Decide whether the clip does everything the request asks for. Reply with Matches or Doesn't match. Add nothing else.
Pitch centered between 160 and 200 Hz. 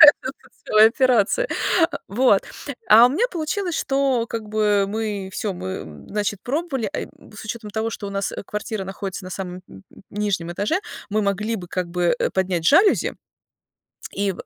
Doesn't match